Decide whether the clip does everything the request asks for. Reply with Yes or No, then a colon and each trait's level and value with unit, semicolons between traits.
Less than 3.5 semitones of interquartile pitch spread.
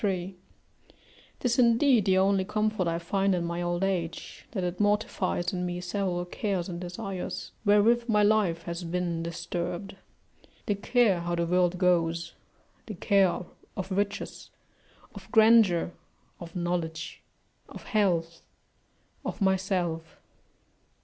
Yes: average, 2.9 semitones